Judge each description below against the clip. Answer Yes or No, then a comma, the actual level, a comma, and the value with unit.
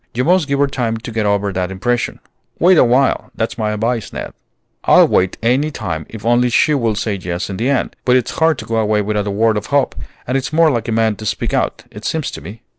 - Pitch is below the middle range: Yes, low, 115 Hz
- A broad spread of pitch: No, average, 3.7 semitones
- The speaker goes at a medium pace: No, fast, 250 wpm